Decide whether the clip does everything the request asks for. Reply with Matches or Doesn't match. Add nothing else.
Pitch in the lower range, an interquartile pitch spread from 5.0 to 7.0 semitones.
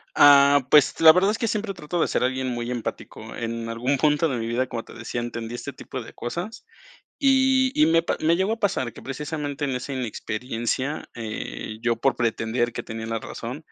Matches